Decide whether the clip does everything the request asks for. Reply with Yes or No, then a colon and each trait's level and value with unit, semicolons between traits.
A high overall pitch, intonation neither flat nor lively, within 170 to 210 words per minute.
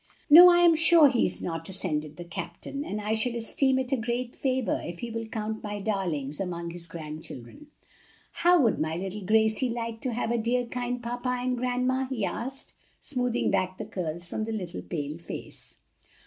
No: high, 225 Hz; wide, 5.9 semitones; average, 190 wpm